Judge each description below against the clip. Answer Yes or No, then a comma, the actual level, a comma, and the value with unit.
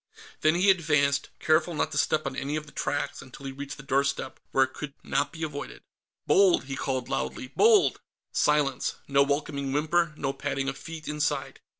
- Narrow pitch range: Yes, narrow, 2.3 semitones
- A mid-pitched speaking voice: Yes, medium, 145 Hz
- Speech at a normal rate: Yes, average, 190 wpm